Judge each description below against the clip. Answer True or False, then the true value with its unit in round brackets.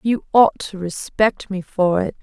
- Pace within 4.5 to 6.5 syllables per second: False (4.0 syllables/s)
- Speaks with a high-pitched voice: True (195 Hz)